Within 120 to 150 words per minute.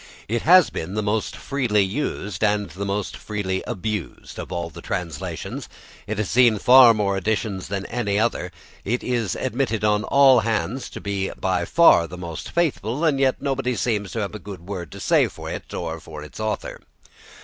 No: average, 190 wpm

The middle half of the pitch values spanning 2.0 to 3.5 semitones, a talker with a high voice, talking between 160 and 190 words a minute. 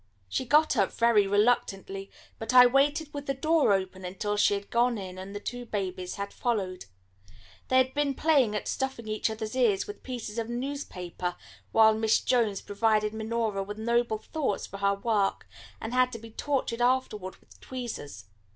No: average, 4.0 semitones; high, 220 Hz; average, 180 wpm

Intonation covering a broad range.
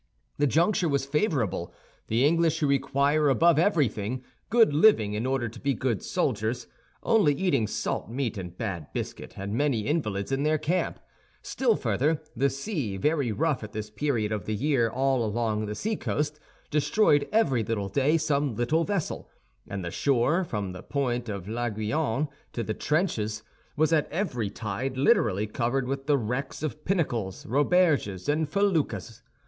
Yes: wide, 6.0 semitones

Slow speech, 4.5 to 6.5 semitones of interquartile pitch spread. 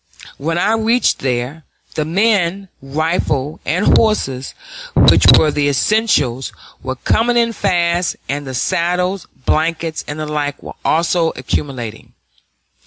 Yes: slow, 125 wpm; average, 5.2 semitones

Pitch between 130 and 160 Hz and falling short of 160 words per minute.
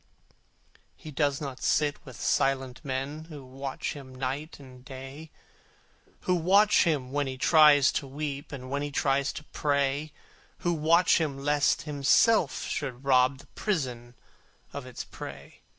Yes: medium, 140 Hz; average, 150 wpm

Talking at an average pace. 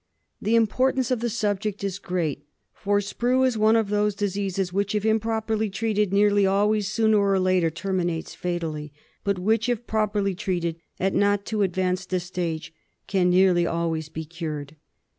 Yes: average, 160 wpm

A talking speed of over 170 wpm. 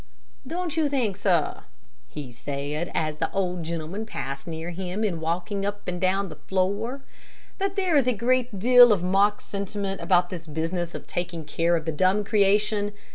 Yes: average, 180 wpm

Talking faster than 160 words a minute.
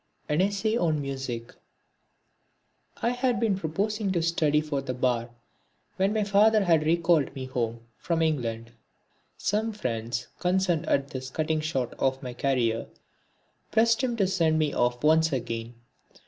No: average, 150 wpm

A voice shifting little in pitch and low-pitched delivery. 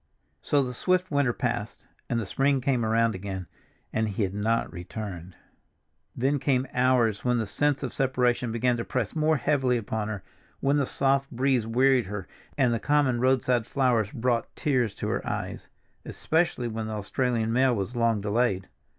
No: average, 3.3 semitones; low, 120 Hz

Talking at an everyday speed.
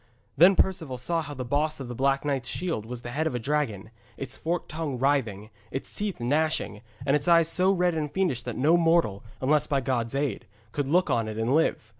No: fast, 220 wpm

